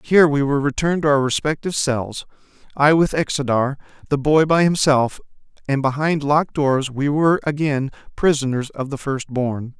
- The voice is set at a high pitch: No, medium, 145 Hz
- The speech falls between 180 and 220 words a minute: No, average, 165 wpm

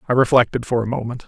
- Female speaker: No, male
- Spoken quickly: Yes, fast, 235 wpm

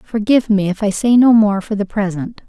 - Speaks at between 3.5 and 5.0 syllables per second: No, 5.4 syllables/s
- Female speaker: Yes, female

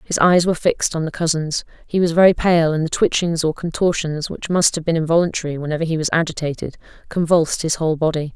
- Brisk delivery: Yes, fast, 210 wpm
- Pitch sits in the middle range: Yes, medium, 160 Hz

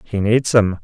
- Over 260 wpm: No, fast, 215 wpm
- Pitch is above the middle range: No, low, 105 Hz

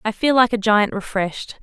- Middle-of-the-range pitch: No, high, 215 Hz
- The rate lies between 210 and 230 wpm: Yes, fast, 220 wpm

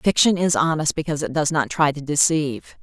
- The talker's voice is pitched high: No, medium, 155 Hz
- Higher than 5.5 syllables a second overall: Yes, 5.8 syllables/s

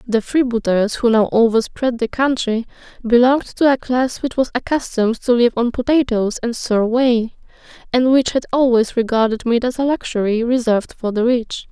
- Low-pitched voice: No, high, 240 Hz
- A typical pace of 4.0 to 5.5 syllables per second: Yes, 5.1 syllables/s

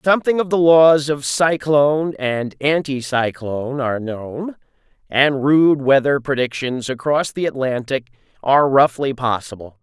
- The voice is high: No, medium, 140 Hz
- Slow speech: Yes, slow, 120 wpm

